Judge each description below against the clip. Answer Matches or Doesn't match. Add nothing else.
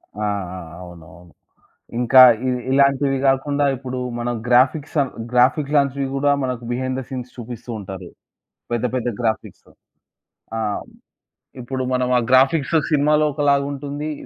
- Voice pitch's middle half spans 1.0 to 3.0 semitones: Matches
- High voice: Doesn't match